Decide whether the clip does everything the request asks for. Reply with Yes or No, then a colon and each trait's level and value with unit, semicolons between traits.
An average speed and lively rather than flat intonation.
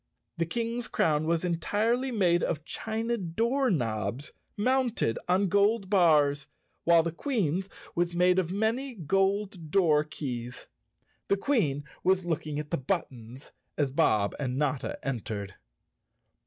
No: slow, 130 wpm; wide, 5.9 semitones